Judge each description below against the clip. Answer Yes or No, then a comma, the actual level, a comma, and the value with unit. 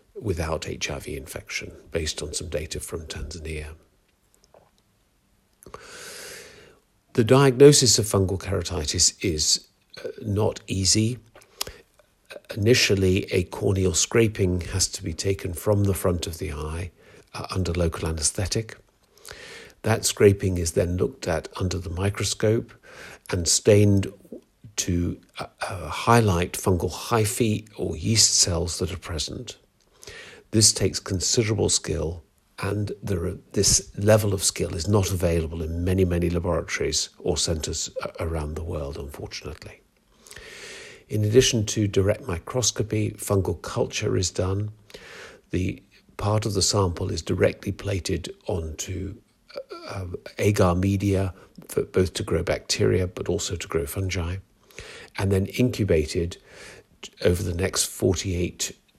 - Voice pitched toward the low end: Yes, very low, 95 Hz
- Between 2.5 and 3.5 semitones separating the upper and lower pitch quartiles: Yes, average, 3.2 semitones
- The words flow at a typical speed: No, slow, 125 wpm